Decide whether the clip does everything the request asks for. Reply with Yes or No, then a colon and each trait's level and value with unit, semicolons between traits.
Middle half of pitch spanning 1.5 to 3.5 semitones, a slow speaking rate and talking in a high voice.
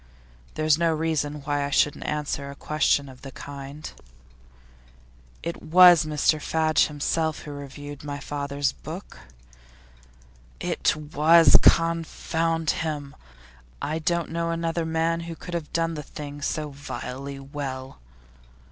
No: narrow, 2.4 semitones; slow, 130 wpm; medium, 150 Hz